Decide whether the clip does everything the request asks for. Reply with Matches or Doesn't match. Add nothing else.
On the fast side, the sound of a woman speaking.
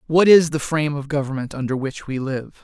Doesn't match